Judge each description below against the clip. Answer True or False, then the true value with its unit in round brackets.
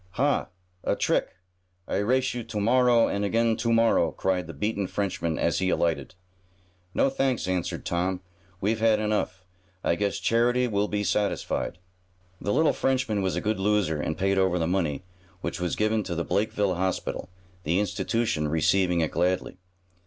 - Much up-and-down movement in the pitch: False (3.8 semitones)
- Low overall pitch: True (100 Hz)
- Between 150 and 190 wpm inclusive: True (165 wpm)